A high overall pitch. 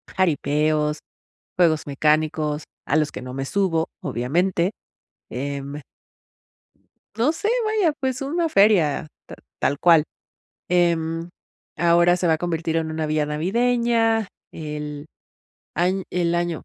No: medium, 165 Hz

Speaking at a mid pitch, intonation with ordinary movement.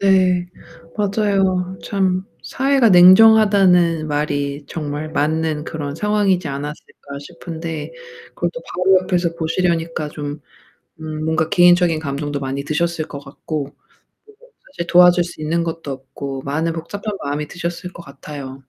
Yes: medium, 165 Hz; average, 3.7 semitones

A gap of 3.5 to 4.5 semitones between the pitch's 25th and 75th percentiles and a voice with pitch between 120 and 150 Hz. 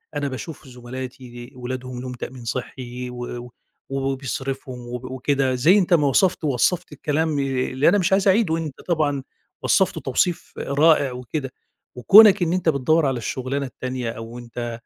Yes: average, 3.9 semitones; low, 135 Hz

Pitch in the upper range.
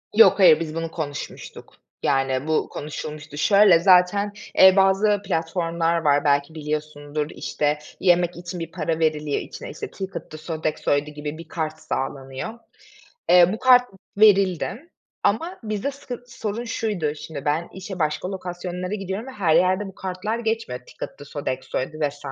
No: medium, 170 Hz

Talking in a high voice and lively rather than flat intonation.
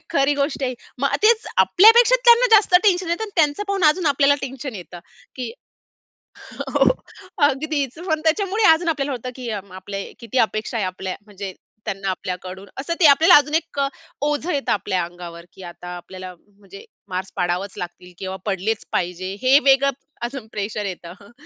Yes: very high, 250 Hz; wide, 8.4 semitones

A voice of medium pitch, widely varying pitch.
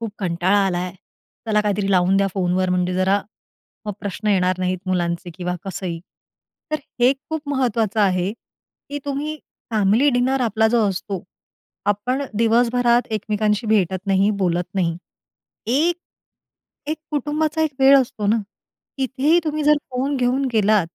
No: high, 210 Hz; wide, 5.8 semitones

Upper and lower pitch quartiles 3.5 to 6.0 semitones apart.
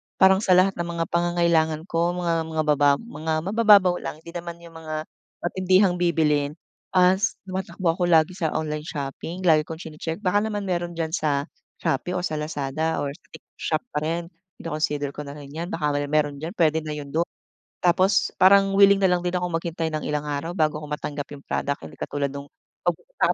No: average, 2.9 semitones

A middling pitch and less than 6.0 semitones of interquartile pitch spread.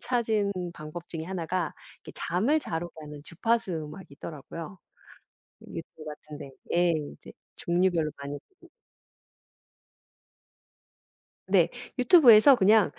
Yes: medium, 175 Hz; wide, 5.5 semitones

